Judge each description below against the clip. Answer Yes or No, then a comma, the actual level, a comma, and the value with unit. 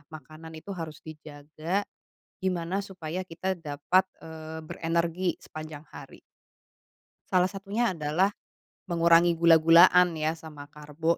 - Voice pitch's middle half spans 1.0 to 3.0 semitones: Yes, narrow, 2.5 semitones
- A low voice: No, medium, 165 Hz